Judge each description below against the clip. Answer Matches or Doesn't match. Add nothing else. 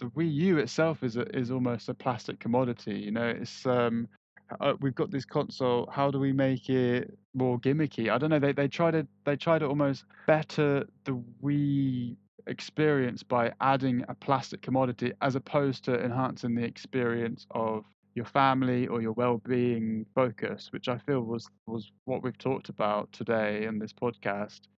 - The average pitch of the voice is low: Matches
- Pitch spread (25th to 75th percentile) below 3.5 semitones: Matches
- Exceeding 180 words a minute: Doesn't match